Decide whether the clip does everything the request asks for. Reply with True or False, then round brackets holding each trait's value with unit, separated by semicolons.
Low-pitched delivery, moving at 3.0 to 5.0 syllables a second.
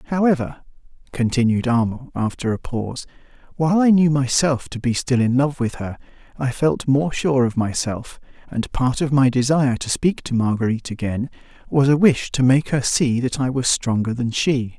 True (130 Hz; 4.5 syllables/s)